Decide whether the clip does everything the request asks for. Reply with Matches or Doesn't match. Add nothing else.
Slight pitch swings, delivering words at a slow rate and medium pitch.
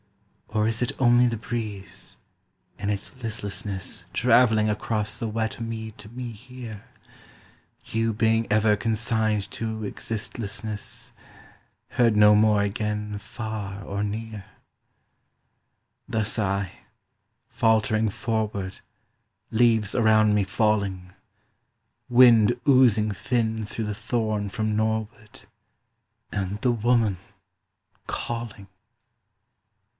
Doesn't match